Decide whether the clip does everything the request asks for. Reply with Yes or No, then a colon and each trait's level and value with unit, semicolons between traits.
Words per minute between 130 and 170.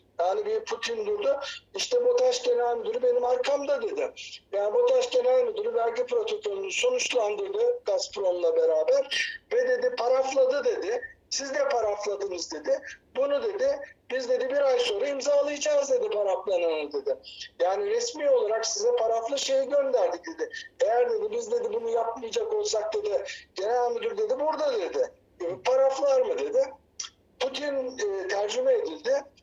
Yes: fast, 140 wpm